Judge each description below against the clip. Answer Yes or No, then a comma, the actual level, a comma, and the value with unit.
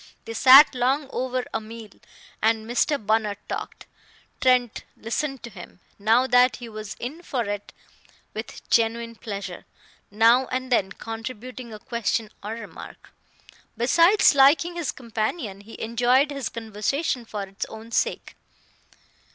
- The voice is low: No, high, 235 Hz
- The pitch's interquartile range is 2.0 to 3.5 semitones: Yes, average, 2.9 semitones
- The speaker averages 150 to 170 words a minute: No, slow, 135 wpm